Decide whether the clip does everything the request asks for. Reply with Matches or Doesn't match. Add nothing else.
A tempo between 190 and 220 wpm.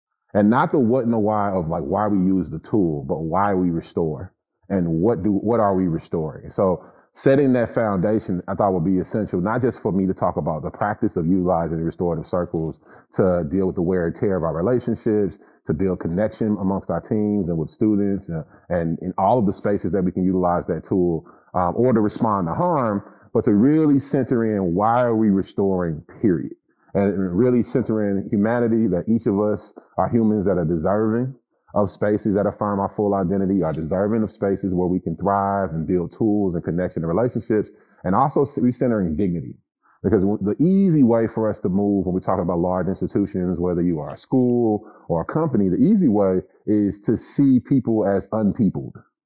Matches